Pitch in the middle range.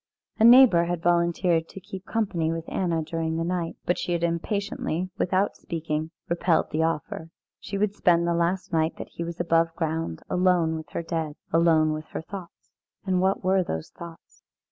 Yes: medium, 170 Hz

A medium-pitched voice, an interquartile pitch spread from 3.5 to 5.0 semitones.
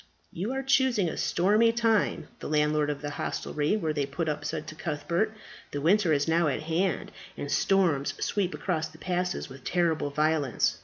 Yes: medium, 160 Hz; average, 4.5 semitones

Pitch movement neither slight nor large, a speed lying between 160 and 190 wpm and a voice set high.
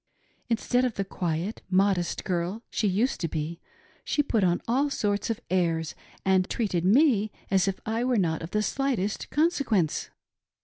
Yes: average, 4.7 semitones; average, 165 wpm; high, 200 Hz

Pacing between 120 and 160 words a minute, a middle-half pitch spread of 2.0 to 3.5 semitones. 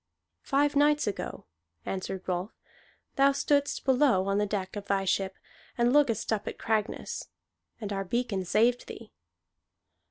No: average, 140 wpm; wide, 5.5 semitones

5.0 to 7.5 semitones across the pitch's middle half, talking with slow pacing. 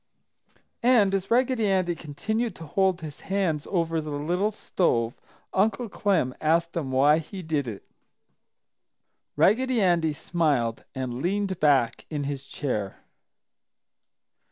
Yes: wide, 5.4 semitones; slow, 125 wpm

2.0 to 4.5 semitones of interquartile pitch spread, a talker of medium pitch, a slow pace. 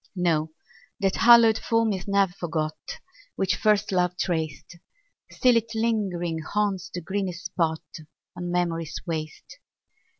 Yes: average, 3.9 semitones; medium, 180 Hz; slow, 125 wpm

